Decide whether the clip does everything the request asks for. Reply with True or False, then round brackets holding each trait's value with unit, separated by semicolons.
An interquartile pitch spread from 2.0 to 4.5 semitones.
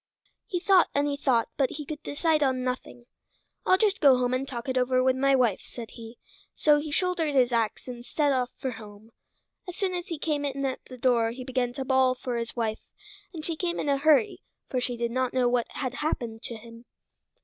True (3.3 semitones)